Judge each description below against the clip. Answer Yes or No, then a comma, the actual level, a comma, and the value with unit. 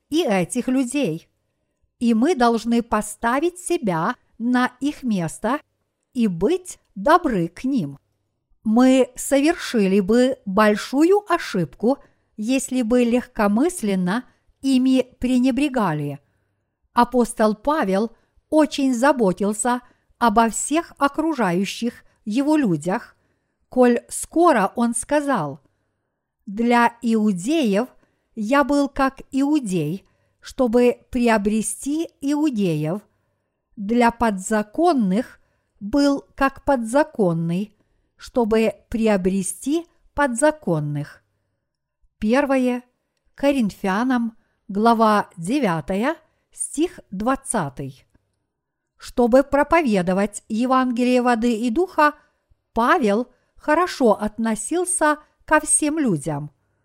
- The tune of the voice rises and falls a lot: Yes, wide, 5.7 semitones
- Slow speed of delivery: Yes, slow, 80 wpm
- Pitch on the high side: Yes, high, 240 Hz